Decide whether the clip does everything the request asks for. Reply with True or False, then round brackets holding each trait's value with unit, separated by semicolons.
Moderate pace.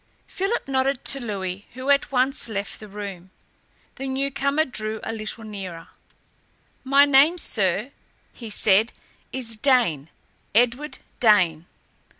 False (125 wpm)